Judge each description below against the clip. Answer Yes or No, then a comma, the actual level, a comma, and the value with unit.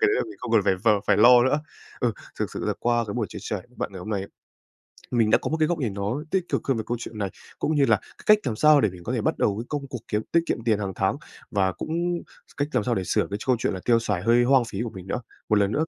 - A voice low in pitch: Yes, low, 115 Hz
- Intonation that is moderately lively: Yes, average, 4.8 semitones